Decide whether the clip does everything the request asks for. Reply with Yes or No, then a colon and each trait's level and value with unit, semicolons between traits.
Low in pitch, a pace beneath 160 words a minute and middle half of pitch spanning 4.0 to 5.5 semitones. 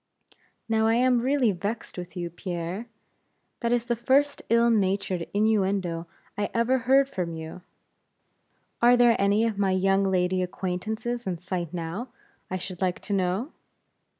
No: high, 200 Hz; average, 150 wpm; average, 4.6 semitones